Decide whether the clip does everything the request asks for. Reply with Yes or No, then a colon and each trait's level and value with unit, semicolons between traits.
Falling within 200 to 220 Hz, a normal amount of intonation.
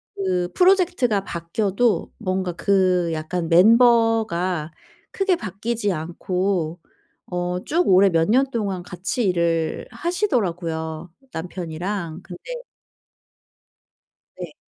No: medium, 185 Hz; average, 4.7 semitones